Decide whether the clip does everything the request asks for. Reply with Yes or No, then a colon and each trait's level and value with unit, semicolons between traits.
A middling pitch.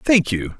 Yes: medium, 145 Hz